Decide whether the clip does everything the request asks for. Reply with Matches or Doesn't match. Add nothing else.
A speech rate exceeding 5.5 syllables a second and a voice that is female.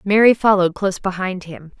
Matches